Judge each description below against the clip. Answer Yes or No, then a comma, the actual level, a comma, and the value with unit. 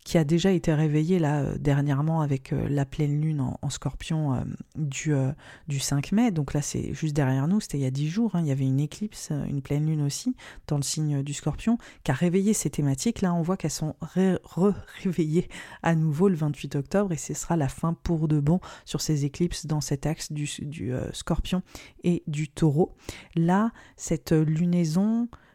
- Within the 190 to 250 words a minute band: Yes, average, 215 wpm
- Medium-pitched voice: Yes, medium, 155 Hz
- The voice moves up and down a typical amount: Yes, average, 3.4 semitones